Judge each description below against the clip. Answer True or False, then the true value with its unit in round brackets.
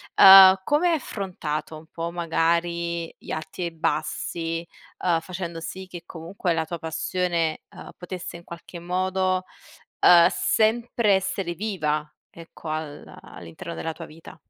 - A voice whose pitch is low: False (170 Hz)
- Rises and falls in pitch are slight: True (2.3 semitones)